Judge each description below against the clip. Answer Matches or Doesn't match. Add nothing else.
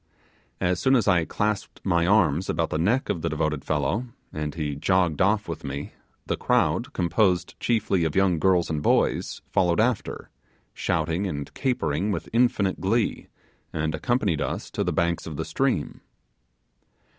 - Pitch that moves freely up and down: Doesn't match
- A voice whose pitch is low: Matches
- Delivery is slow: Doesn't match